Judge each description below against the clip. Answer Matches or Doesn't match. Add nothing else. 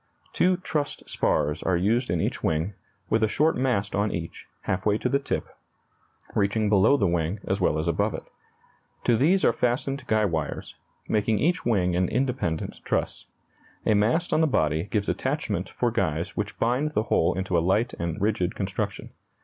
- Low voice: Matches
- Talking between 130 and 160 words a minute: Doesn't match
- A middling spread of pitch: Doesn't match